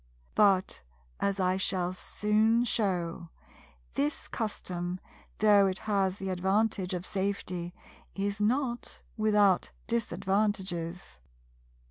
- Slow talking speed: Yes, slow, 95 wpm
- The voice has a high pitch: Yes, high, 195 Hz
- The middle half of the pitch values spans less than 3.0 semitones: Yes, narrow, 2.5 semitones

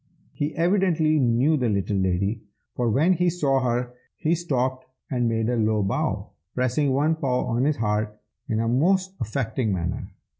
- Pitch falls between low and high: No, low, 125 Hz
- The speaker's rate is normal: Yes, average, 165 wpm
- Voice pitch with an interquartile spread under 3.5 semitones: No, wide, 5.6 semitones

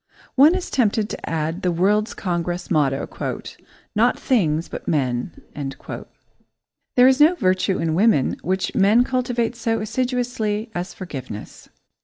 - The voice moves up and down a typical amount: No, wide, 6.3 semitones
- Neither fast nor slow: No, slow, 130 wpm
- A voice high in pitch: Yes, high, 205 Hz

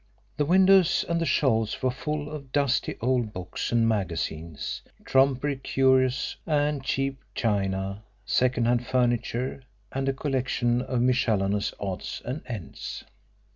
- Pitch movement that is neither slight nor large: Yes, average, 3.6 semitones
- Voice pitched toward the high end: No, low, 125 Hz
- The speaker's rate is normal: No, slow, 130 wpm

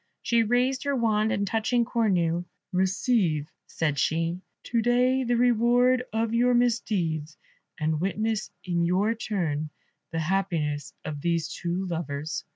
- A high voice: Yes, high, 195 Hz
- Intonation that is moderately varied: No, wide, 6.2 semitones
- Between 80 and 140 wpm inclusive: Yes, slow, 135 wpm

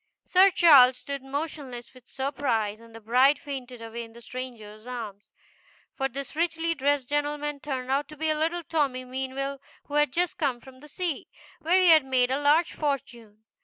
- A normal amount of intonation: Yes, average, 3.1 semitones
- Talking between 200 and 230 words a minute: No, average, 175 wpm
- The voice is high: Yes, very high, 270 Hz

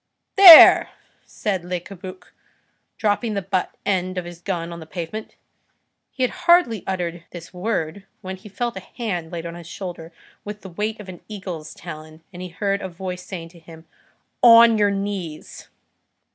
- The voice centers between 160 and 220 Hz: Yes, medium, 185 Hz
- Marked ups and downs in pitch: No, average, 3.2 semitones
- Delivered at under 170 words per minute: No, average, 175 wpm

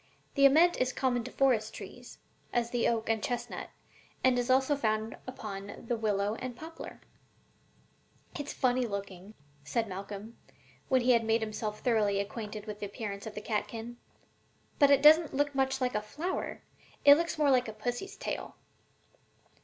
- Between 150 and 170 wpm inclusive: Yes, average, 165 wpm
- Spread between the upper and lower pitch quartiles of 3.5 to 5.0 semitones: Yes, average, 3.8 semitones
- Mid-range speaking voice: No, high, 235 Hz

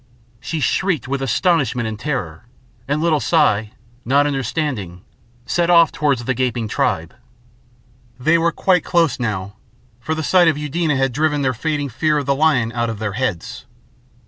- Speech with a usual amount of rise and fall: Yes, average, 5.0 semitones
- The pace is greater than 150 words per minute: Yes, average, 165 wpm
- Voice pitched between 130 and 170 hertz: Yes, medium, 140 Hz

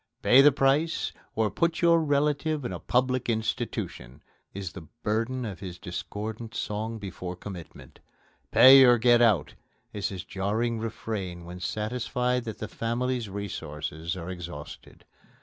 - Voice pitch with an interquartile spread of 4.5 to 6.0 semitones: Yes, average, 5.1 semitones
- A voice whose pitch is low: Yes, low, 110 Hz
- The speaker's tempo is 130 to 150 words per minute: Yes, average, 140 wpm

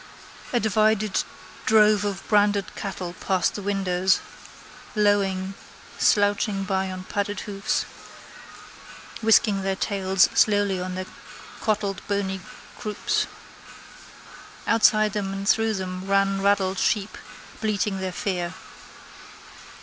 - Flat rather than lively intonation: Yes, narrow, 1.6 semitones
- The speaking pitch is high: Yes, high, 195 Hz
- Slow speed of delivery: Yes, slow, 105 wpm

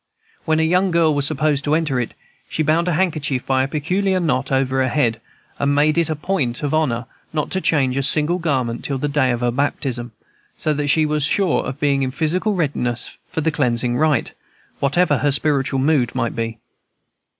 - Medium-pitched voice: Yes, medium, 145 Hz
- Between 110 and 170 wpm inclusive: No, fast, 205 wpm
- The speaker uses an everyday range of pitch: Yes, average, 3.2 semitones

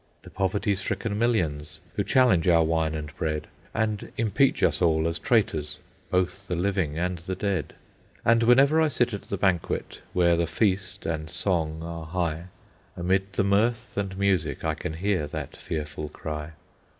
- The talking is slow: No, average, 165 wpm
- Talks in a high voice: No, very low, 90 Hz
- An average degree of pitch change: Yes, average, 4.1 semitones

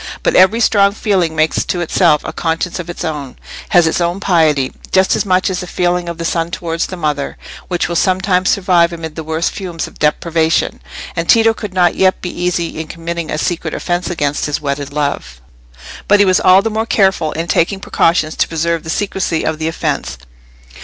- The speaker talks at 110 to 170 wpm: No, average, 200 wpm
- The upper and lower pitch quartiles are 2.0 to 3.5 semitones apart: Yes, narrow, 2.6 semitones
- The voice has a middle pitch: Yes, medium, 170 Hz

